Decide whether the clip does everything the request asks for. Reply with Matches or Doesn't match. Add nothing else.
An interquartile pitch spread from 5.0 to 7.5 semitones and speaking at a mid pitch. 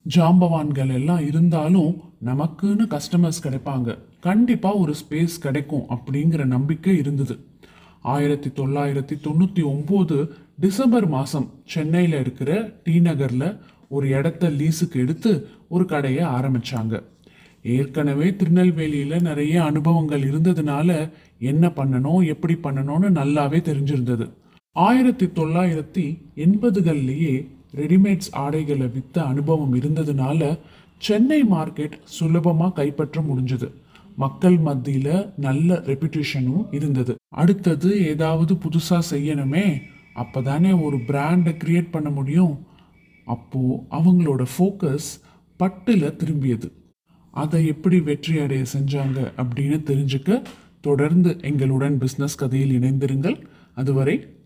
Doesn't match